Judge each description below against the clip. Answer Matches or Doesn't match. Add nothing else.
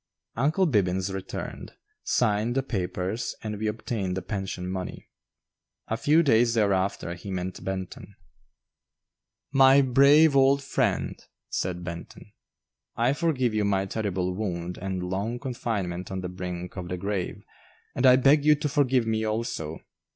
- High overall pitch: Doesn't match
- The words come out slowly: Doesn't match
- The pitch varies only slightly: Doesn't match